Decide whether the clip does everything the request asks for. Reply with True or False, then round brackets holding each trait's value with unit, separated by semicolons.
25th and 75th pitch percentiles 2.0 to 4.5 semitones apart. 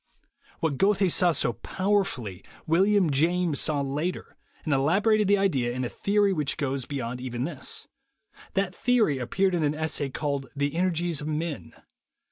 False (5.4 semitones)